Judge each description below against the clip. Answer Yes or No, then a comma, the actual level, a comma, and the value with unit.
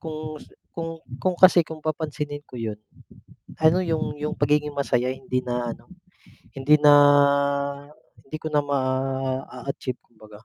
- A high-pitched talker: No, medium, 145 Hz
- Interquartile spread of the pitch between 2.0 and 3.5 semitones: Yes, average, 3.1 semitones